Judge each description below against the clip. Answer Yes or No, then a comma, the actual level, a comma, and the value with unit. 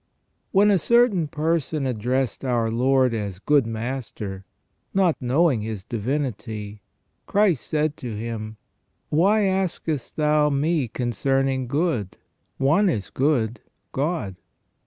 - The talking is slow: Yes, slow, 120 wpm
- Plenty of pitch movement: Yes, wide, 5.7 semitones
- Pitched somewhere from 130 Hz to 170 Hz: Yes, low, 135 Hz